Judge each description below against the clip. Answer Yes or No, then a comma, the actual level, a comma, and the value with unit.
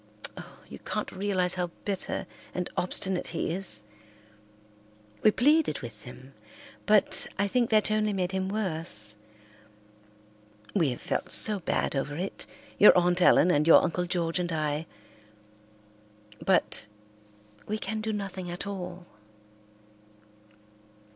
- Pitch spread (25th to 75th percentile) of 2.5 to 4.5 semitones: Yes, average, 3.6 semitones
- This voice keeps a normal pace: No, slow, 130 wpm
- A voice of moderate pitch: Yes, medium, 180 Hz